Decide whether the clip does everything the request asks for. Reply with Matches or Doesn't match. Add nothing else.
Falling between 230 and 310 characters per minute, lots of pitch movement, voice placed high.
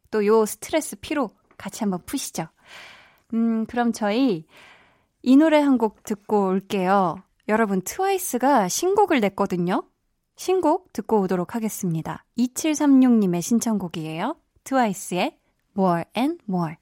Matches